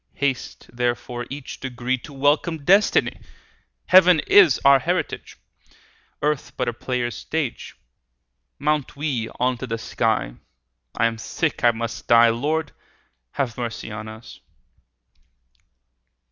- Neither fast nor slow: No, slow, 125 wpm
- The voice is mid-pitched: No, low, 125 Hz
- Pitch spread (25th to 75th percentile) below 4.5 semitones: Yes, average, 3.8 semitones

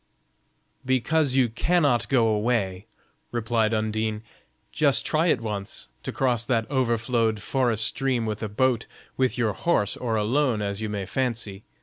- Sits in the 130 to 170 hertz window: No, low, 115 Hz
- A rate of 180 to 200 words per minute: No, average, 145 wpm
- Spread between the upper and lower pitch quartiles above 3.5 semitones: No, average, 3.2 semitones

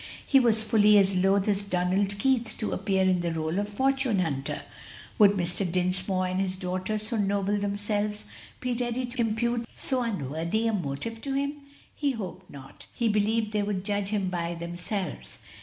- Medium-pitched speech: No, high, 205 Hz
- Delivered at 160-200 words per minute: Yes, average, 175 wpm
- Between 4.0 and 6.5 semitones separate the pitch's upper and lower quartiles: No, average, 3.4 semitones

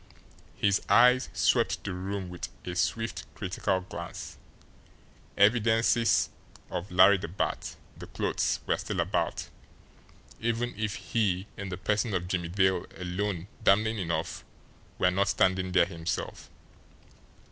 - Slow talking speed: Yes, slow, 125 wpm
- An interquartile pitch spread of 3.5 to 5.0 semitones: No, average, 3.0 semitones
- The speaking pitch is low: Yes, very low, 95 Hz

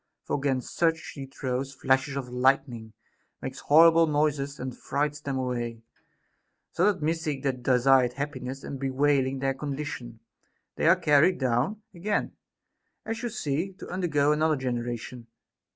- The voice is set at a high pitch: No, medium, 140 Hz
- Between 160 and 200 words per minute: No, average, 140 wpm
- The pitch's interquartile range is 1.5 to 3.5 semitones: Yes, average, 3.0 semitones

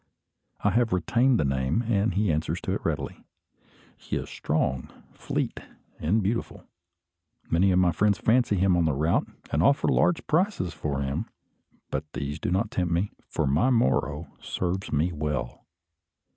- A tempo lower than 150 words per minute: No, average, 160 wpm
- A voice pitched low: Yes, very low, 90 Hz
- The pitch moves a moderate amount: No, wide, 6.0 semitones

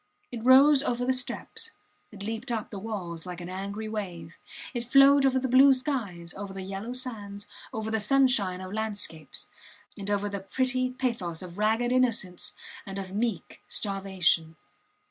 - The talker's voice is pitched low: No, high, 215 Hz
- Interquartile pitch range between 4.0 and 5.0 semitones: Yes, average, 4.7 semitones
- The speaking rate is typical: Yes, average, 165 wpm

